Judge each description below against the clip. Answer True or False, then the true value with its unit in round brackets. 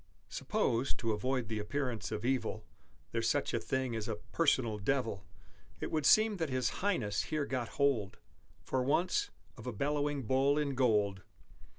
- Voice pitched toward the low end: True (130 Hz)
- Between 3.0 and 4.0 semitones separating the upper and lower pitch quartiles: False (4.4 semitones)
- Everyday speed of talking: True (165 wpm)